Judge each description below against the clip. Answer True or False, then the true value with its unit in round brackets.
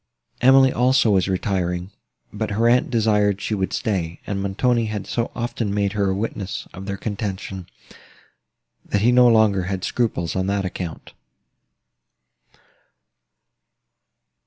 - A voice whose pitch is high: False (100 Hz)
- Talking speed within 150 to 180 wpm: False (135 wpm)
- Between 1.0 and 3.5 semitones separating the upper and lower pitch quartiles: True (3.2 semitones)